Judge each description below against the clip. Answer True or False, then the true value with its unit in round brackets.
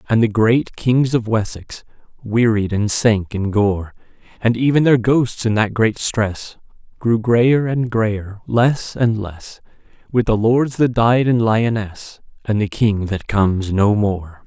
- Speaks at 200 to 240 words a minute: False (165 wpm)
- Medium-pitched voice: False (110 Hz)